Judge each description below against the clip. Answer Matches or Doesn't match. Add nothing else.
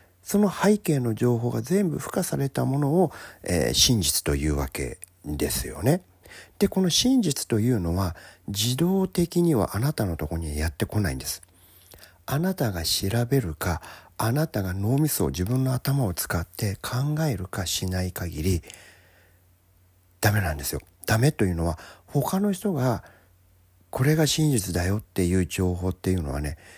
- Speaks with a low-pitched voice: Matches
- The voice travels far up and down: Matches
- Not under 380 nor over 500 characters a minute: Doesn't match